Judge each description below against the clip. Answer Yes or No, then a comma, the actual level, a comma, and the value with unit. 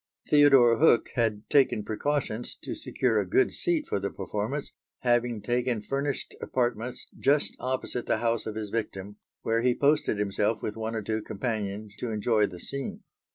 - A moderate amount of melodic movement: Yes, average, 3.4 semitones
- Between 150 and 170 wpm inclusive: Yes, average, 165 wpm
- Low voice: Yes, low, 115 Hz